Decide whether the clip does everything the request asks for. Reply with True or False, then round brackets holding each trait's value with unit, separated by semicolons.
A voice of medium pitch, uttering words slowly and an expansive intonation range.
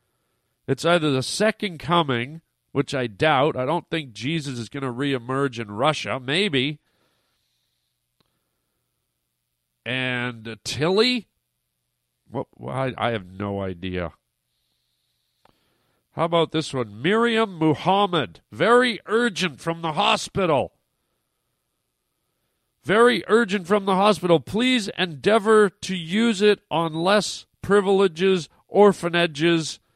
True (160 Hz; 105 wpm; 8.1 semitones)